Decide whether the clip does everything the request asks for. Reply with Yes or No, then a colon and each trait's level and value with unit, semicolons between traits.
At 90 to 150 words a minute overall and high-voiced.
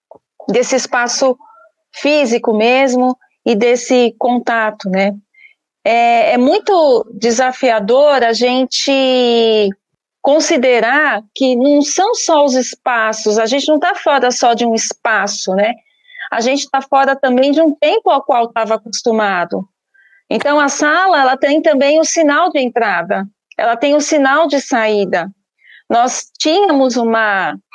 Yes: average, 140 wpm; very high, 255 Hz